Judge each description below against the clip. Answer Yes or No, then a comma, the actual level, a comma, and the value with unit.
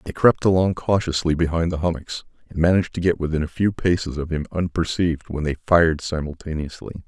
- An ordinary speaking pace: Yes, average, 185 wpm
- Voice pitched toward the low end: Yes, very low, 80 Hz